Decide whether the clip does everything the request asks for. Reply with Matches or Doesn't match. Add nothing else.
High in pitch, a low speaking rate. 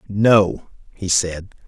Doesn't match